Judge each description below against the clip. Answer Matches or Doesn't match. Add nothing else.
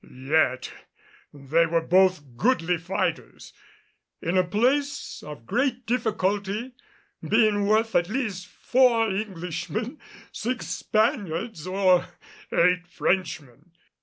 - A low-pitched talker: Doesn't match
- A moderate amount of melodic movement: Matches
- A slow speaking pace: Matches